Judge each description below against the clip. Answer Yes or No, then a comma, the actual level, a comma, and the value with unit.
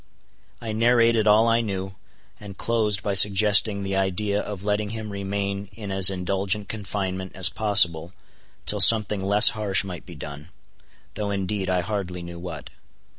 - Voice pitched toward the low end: Yes, low, 100 Hz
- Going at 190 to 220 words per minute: No, average, 150 wpm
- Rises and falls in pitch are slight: Yes, narrow, 1.9 semitones